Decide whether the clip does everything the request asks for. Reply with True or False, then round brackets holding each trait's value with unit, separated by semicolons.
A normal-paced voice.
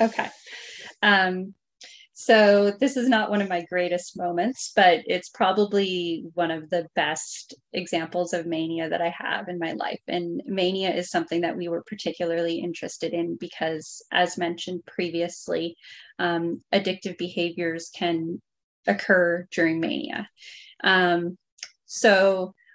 False (130 wpm)